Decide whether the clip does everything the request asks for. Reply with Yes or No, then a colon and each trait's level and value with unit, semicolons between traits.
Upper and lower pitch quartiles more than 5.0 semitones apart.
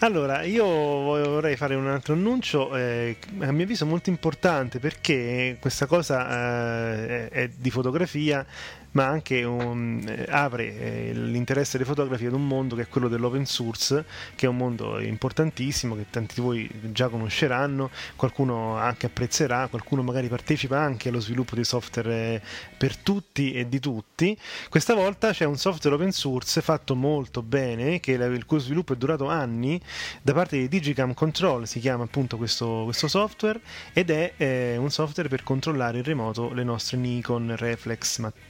No: average, 4.0 semitones